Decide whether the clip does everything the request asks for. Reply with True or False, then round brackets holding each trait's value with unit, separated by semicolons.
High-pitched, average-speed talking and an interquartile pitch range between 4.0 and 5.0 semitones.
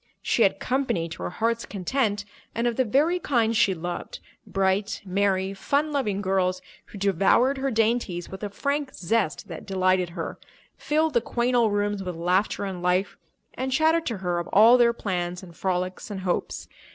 True (200 Hz; 175 wpm; 4.6 semitones)